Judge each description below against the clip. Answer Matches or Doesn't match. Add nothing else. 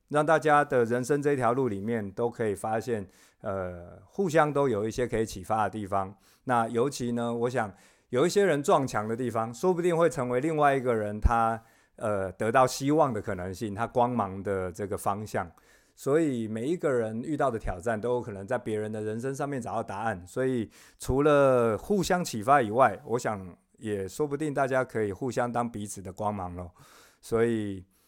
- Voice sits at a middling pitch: Doesn't match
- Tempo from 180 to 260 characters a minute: Doesn't match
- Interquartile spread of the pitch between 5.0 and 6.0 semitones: Doesn't match